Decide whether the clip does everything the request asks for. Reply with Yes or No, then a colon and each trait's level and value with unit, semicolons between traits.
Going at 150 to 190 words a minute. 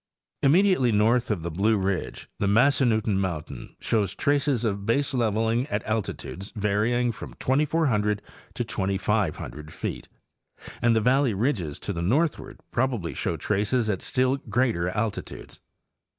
No: slow, 135 wpm